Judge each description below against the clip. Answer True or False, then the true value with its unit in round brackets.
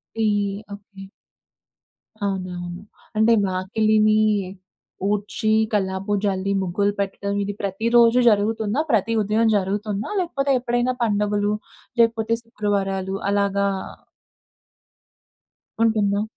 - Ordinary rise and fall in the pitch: False (2.1 semitones)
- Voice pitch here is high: True (205 Hz)